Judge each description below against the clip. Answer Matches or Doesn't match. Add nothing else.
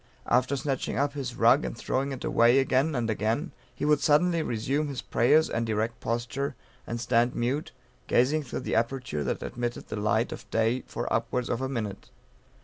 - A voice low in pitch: Matches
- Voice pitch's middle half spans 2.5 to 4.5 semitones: Matches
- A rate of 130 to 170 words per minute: Doesn't match